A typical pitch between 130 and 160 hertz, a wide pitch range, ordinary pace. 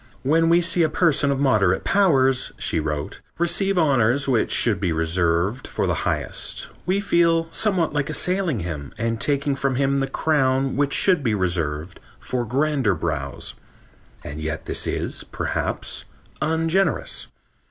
Yes: low, 135 Hz; wide, 7.9 semitones; average, 150 wpm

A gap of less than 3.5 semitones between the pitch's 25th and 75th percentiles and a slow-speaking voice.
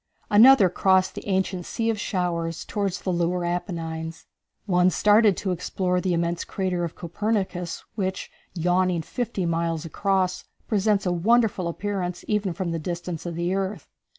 No: narrow, 2.5 semitones; average, 150 wpm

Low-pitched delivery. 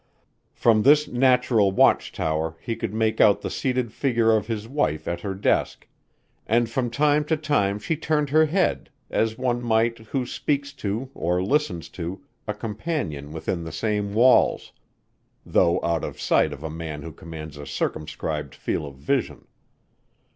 Yes: low, 110 Hz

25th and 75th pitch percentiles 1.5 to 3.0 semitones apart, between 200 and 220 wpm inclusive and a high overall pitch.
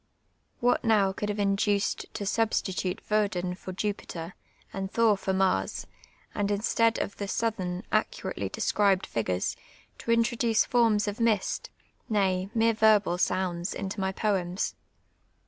No: narrow, 2.6 semitones; slow, 135 wpm; high, 200 Hz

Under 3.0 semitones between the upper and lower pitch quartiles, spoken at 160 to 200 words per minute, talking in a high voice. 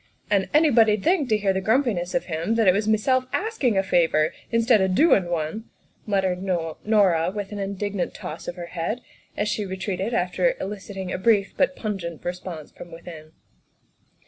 No: average, 3.8 semitones; average, 175 wpm; high, 195 Hz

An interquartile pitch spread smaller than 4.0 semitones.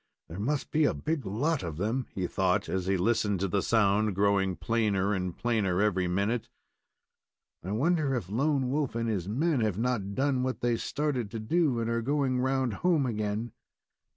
No: average, 5.0 semitones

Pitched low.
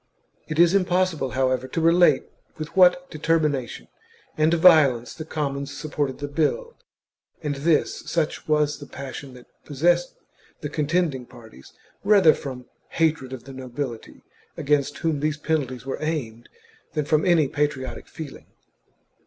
No: medium, 150 Hz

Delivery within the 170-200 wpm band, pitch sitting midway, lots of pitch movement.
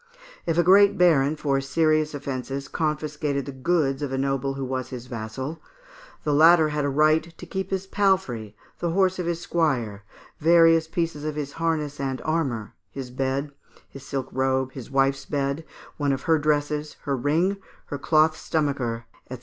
No: average, 175 wpm; medium, 145 Hz; average, 3.2 semitones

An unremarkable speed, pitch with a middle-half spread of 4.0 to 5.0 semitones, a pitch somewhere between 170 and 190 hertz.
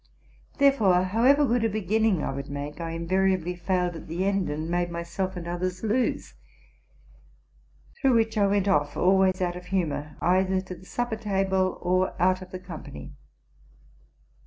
No: average, 160 wpm; narrow, 2.4 semitones; medium, 185 Hz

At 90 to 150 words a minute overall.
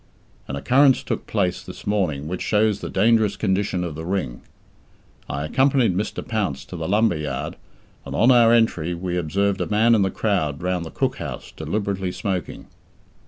No: average, 175 wpm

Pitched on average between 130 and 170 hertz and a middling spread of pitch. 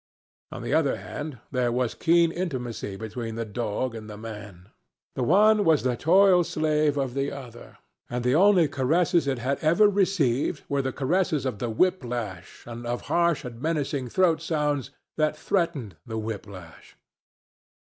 No: low, 135 Hz; wide, 5.8 semitones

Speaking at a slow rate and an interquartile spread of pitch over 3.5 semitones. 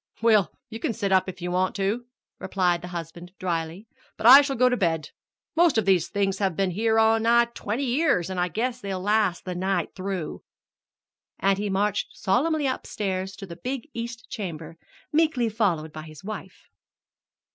No: average, 185 wpm; average, 4.4 semitones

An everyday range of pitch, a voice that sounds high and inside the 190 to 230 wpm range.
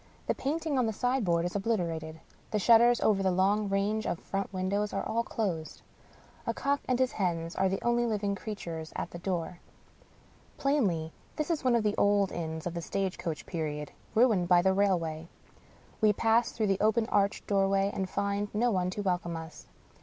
Yes: average, 4.0 semitones; high, 195 Hz; average, 195 wpm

